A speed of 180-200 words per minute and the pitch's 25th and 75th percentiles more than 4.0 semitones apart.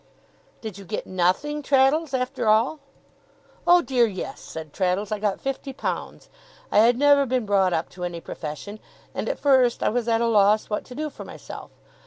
Yes: average, 190 wpm; average, 5.2 semitones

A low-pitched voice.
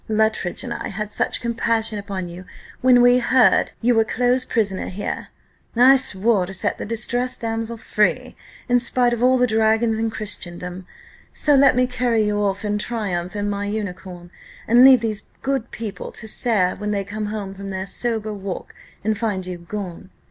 No: high, 215 Hz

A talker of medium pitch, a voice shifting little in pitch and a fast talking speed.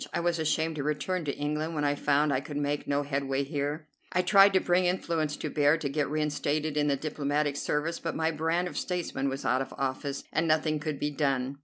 Yes: medium, 150 Hz; narrow, 2.1 semitones; fast, 225 wpm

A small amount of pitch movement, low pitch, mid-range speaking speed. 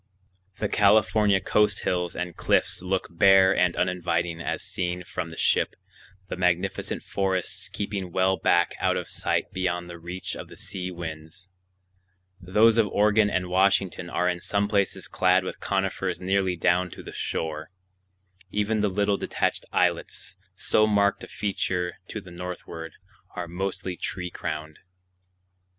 Yes: narrow, 2.1 semitones; very low, 90 Hz; average, 150 wpm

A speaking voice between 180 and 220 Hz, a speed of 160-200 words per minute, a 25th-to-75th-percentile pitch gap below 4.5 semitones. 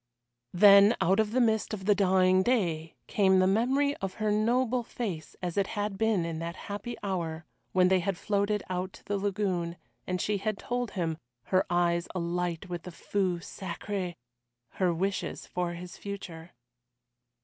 Yes: high, 190 Hz; average, 170 wpm; average, 3.0 semitones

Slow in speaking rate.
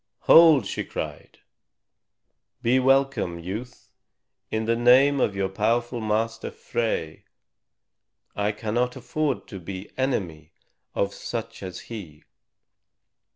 Yes: slow, 110 wpm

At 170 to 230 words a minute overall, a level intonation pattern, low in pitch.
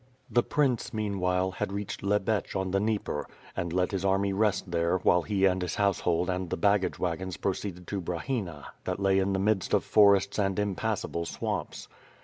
Yes: average, 185 wpm; narrow, 2.0 semitones; very low, 95 Hz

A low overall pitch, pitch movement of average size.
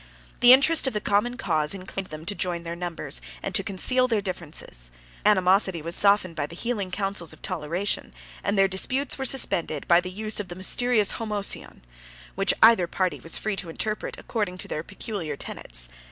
No: high, 190 Hz; average, 4.0 semitones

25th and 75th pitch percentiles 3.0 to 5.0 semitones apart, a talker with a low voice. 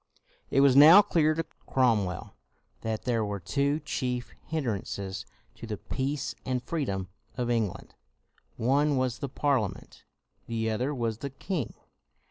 Yes: average, 4.3 semitones; low, 125 Hz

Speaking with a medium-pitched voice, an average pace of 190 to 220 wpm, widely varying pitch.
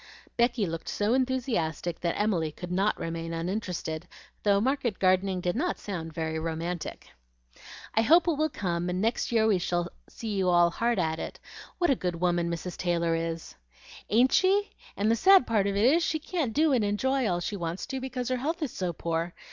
No: high, 195 Hz; average, 200 wpm; wide, 6.5 semitones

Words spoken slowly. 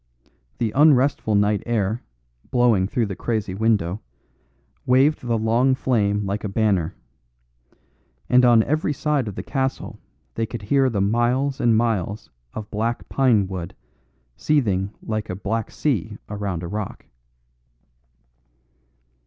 Yes: slow, 130 wpm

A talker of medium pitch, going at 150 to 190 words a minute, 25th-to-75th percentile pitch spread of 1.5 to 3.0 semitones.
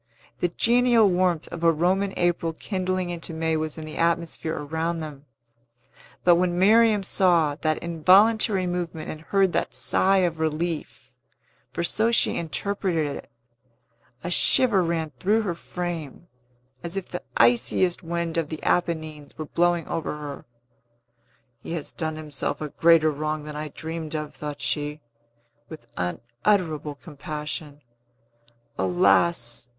No: medium, 165 Hz; average, 140 wpm; average, 2.7 semitones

